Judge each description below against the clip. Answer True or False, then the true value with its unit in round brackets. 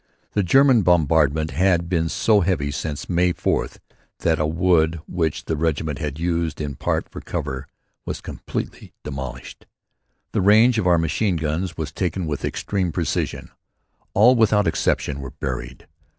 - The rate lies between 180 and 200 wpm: False (150 wpm)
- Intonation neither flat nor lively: True (3.6 semitones)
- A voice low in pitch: True (80 Hz)